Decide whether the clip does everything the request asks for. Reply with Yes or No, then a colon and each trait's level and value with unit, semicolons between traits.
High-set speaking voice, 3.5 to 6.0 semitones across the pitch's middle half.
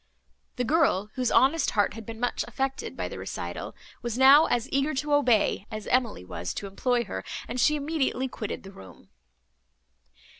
Yes: high, 245 Hz; average, 4.3 semitones